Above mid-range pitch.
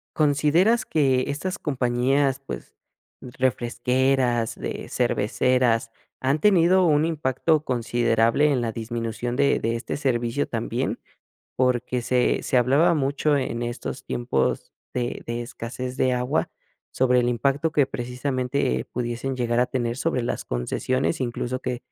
No: low, 125 Hz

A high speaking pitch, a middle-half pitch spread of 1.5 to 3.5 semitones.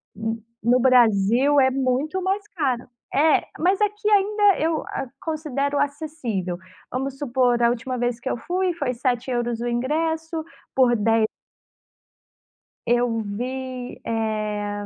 No: very high, 255 Hz; average, 4.7 semitones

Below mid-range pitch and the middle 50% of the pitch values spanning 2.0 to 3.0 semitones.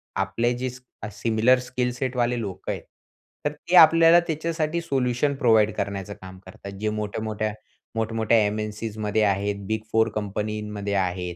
No: low, 110 Hz; average, 3.5 semitones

